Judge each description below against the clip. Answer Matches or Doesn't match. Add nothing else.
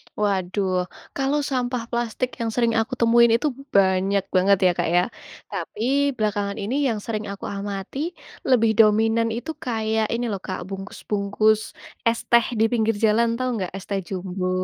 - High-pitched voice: Matches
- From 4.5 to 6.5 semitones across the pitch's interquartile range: Doesn't match